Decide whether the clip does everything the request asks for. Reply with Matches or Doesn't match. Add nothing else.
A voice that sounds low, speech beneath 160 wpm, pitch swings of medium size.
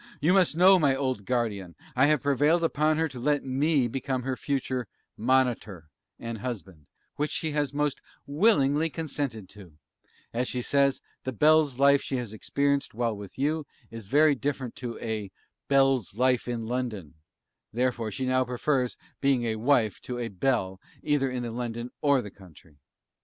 Doesn't match